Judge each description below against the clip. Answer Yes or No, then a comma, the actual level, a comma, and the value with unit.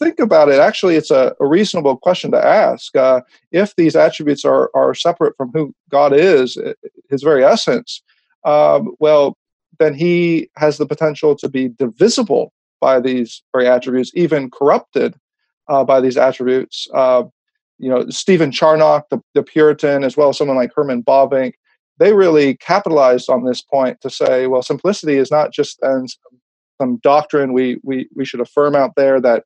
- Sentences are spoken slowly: No, average, 170 wpm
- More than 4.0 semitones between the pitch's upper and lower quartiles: No, average, 3.6 semitones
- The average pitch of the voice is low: No, medium, 145 Hz